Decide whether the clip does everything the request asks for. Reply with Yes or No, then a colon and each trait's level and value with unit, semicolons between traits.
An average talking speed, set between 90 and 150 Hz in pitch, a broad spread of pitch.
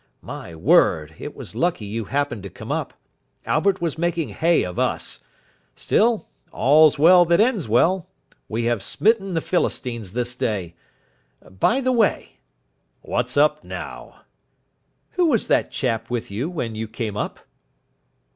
Yes: average, 150 wpm; medium, 140 Hz; wide, 8.1 semitones